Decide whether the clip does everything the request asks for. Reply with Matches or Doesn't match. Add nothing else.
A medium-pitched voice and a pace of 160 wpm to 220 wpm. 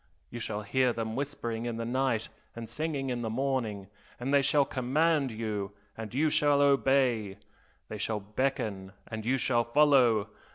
Doesn't match